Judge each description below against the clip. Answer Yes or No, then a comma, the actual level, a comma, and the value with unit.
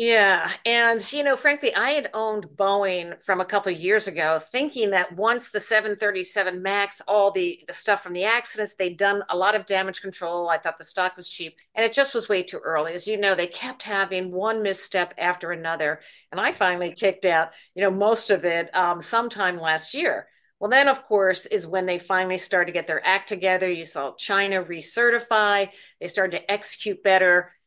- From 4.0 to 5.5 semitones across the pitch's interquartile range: No, average, 3.1 semitones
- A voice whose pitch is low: No, high, 195 Hz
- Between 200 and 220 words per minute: Yes, fast, 205 wpm